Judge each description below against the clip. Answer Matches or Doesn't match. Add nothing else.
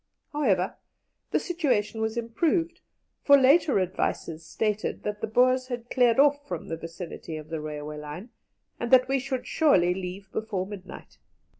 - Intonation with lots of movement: Matches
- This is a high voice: Matches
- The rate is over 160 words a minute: Doesn't match